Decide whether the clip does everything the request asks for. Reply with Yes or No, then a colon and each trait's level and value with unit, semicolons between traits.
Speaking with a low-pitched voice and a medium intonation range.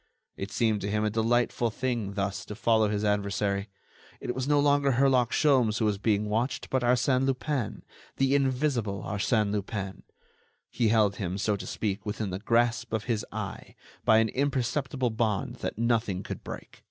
Yes: low, 110 Hz; average, 3.5 semitones